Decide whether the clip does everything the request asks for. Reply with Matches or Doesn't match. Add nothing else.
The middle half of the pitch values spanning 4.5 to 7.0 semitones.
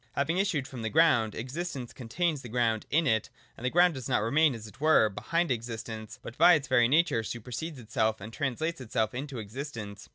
Matches